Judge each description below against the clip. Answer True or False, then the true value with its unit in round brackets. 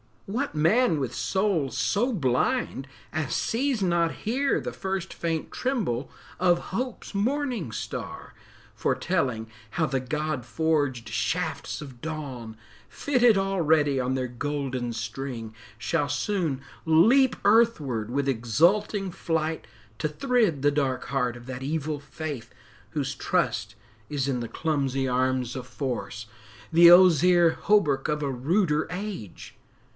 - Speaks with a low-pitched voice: False (150 Hz)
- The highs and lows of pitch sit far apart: True (6.5 semitones)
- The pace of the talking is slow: True (130 wpm)